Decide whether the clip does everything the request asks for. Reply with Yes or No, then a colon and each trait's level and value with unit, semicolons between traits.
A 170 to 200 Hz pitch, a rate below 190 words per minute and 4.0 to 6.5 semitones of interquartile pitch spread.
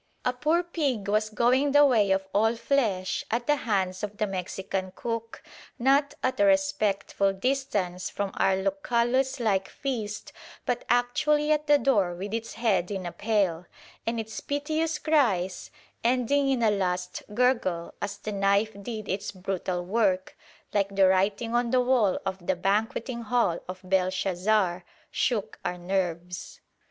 No: high, 210 Hz; average, 155 wpm; average, 4.4 semitones